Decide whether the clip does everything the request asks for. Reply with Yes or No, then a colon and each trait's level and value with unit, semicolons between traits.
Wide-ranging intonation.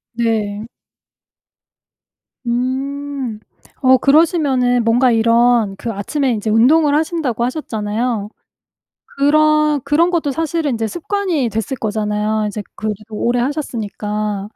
No: average, 5.0 semitones